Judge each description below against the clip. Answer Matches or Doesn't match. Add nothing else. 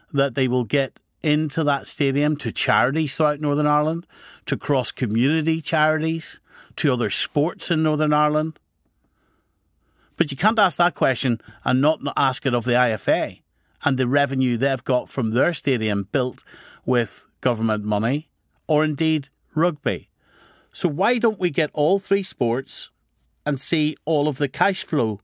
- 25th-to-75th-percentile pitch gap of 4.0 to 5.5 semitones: Doesn't match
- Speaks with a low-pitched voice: Doesn't match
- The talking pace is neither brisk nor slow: Matches